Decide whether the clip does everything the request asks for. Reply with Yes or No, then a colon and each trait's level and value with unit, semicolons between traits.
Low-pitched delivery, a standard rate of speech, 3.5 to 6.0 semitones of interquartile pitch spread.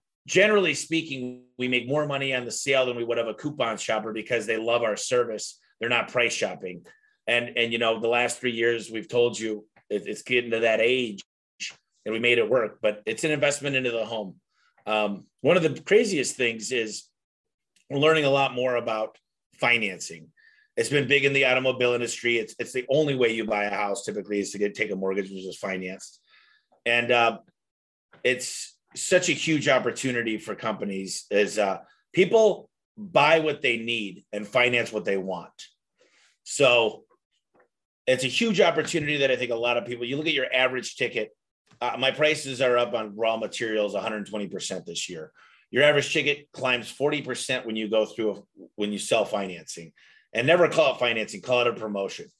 Yes: low, 120 Hz; average, 190 wpm; average, 4.2 semitones